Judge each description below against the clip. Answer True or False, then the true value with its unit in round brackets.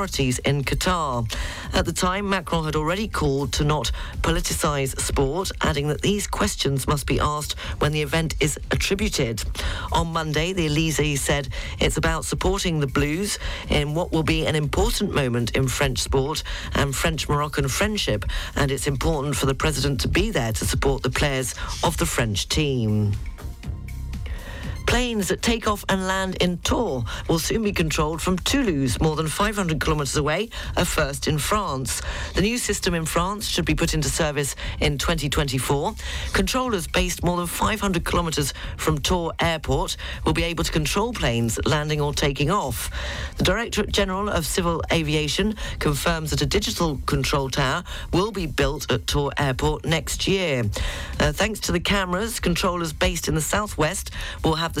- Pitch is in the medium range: True (150 Hz)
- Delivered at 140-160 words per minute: False (170 wpm)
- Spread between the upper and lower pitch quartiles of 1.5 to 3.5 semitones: False (4.6 semitones)